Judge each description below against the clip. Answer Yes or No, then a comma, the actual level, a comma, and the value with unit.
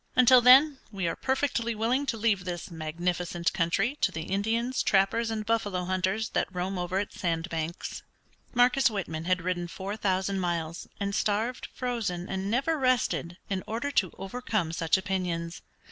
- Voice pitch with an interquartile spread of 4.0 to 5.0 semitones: Yes, average, 4.7 semitones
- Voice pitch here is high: Yes, high, 195 Hz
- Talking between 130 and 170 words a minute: Yes, average, 160 wpm